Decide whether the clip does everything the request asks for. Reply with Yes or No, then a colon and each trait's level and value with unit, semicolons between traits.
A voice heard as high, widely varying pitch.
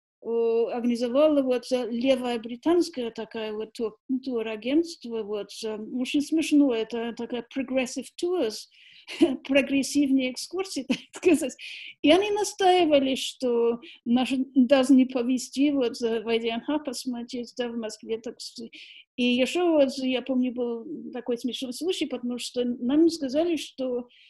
No: very high, 255 Hz; average, 3.2 semitones